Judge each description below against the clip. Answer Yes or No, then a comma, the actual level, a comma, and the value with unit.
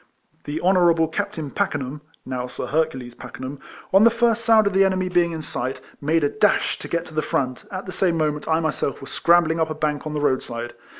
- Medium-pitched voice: Yes, medium, 160 Hz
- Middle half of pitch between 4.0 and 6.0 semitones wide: Yes, average, 4.4 semitones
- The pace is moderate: No, fast, 230 wpm